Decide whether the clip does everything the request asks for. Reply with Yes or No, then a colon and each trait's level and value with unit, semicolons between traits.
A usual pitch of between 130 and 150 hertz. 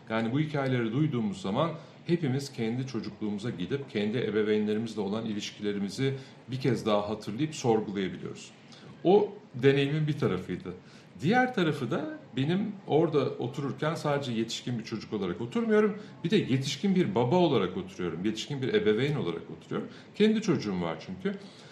Yes: medium, 140 Hz